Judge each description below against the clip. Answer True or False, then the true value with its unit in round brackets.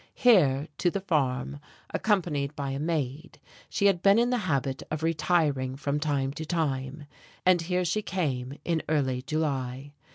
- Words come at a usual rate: True (160 wpm)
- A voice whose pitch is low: False (150 Hz)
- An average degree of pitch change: True (4.3 semitones)